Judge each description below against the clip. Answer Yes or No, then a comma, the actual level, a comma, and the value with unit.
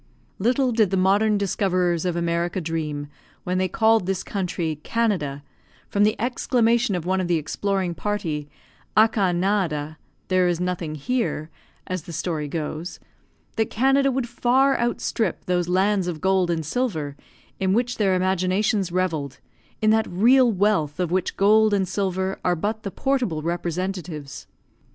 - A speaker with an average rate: Yes, average, 150 wpm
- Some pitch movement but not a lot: Yes, average, 4.1 semitones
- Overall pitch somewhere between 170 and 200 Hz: Yes, medium, 185 Hz